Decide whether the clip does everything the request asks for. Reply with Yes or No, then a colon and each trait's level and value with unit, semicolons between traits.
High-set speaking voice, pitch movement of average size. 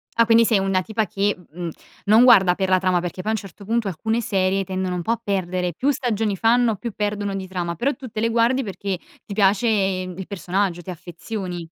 Yes: high, 195 Hz; average, 3.4 semitones